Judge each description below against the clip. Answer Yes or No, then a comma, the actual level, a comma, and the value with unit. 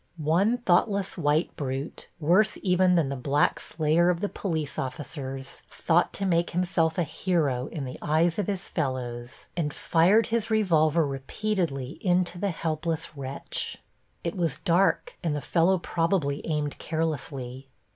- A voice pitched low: No, medium, 165 Hz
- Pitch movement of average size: Yes, average, 4.0 semitones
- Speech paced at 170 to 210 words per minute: No, average, 145 wpm